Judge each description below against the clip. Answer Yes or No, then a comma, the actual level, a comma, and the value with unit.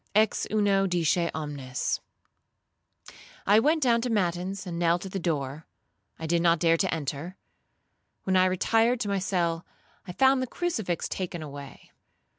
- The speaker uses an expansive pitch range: No, average, 3.7 semitones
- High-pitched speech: No, medium, 180 Hz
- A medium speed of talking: Yes, average, 155 wpm